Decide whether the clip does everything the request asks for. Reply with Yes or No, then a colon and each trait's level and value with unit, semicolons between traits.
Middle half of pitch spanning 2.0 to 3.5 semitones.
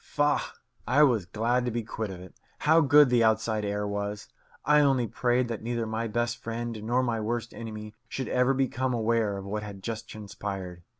Yes: average, 2.8 semitones